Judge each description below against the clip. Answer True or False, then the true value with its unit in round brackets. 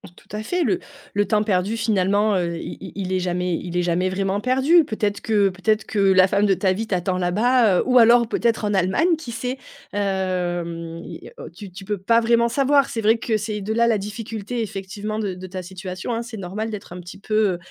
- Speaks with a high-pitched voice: True (205 Hz)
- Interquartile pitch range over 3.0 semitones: True (3.5 semitones)